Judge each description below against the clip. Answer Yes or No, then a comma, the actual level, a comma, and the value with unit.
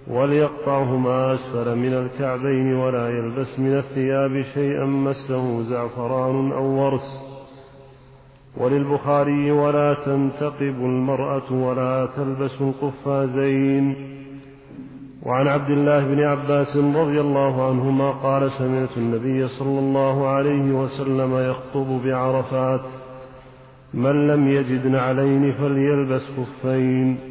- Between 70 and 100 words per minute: Yes, average, 95 wpm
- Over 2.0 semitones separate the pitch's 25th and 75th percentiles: No, narrow, 1.0 semitones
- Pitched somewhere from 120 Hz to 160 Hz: Yes, low, 135 Hz